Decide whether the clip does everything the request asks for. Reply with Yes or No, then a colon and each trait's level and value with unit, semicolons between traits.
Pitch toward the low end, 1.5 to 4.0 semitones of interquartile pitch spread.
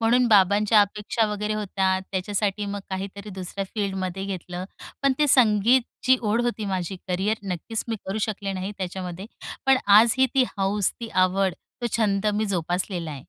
No: high, 200 Hz; narrow, 2.5 semitones